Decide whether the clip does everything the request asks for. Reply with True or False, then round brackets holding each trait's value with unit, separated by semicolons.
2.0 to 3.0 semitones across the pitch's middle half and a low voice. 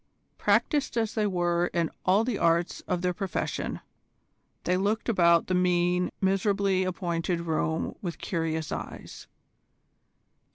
False (2.4 semitones; 180 Hz)